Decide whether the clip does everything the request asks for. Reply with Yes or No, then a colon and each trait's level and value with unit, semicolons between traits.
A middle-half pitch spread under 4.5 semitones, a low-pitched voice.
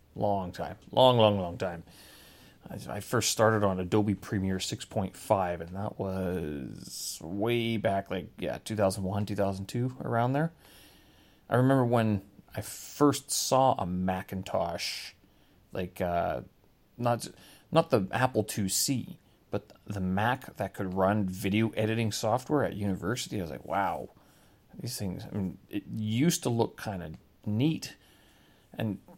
Yes: average, 3.6 semitones; low, 100 Hz